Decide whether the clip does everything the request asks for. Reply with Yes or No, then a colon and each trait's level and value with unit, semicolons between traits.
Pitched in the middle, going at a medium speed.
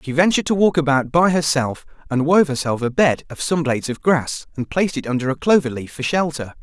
No: medium, 150 Hz; fast, 235 wpm